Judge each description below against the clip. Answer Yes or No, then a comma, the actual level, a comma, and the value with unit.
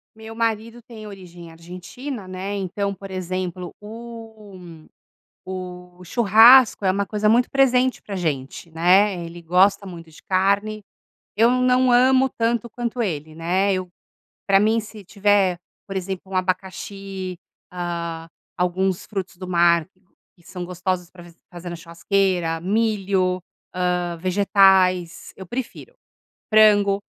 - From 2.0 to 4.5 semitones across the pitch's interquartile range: Yes, average, 3.2 semitones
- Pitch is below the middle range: No, high, 190 Hz